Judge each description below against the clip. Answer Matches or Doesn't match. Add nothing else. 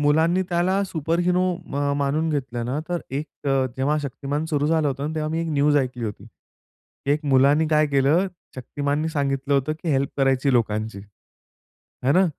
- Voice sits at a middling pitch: Matches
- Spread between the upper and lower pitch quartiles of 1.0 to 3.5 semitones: Matches